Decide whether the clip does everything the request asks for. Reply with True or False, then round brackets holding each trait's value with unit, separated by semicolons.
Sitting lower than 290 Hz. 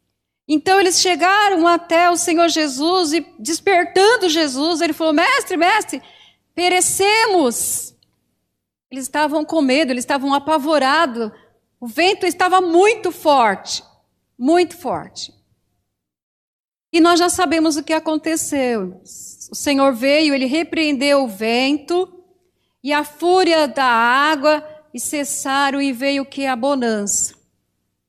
False (315 Hz)